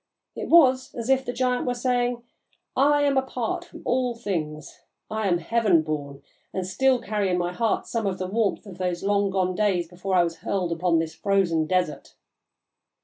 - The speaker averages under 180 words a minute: No, average, 190 wpm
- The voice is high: Yes, high, 200 Hz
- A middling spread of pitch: No, wide, 5.7 semitones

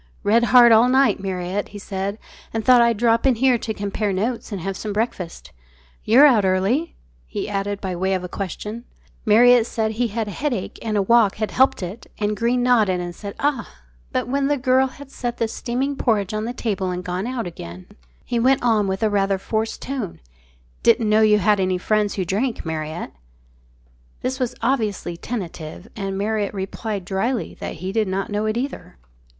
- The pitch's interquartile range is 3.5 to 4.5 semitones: Yes, average, 3.8 semitones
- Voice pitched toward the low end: No, high, 215 Hz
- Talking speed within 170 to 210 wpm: Yes, average, 195 wpm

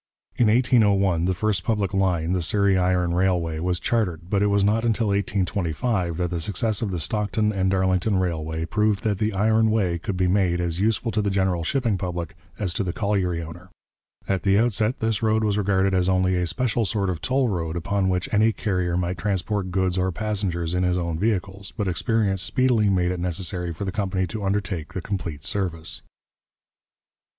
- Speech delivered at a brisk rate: No, average, 195 wpm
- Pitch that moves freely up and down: No, average, 3.0 semitones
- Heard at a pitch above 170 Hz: No, very low, 95 Hz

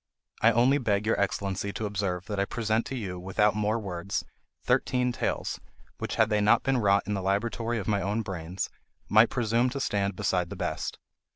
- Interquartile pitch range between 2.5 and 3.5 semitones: Yes, average, 2.8 semitones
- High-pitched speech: No, low, 105 Hz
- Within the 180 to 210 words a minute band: Yes, average, 195 wpm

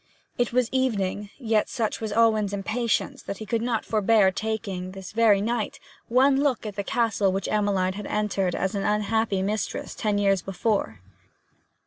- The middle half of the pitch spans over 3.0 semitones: No, narrow, 2.6 semitones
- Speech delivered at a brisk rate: No, average, 160 wpm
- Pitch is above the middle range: Yes, high, 210 Hz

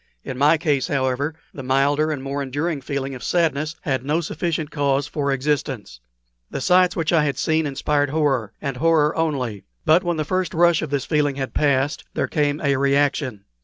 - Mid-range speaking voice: Yes, medium, 145 Hz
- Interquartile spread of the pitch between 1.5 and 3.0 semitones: Yes, narrow, 2.6 semitones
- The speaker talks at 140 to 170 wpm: No, average, 190 wpm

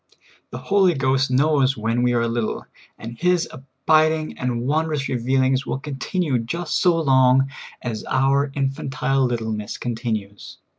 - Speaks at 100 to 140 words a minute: Yes, slow, 135 wpm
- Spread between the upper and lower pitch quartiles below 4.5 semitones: Yes, average, 3.5 semitones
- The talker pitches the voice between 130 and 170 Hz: Yes, low, 135 Hz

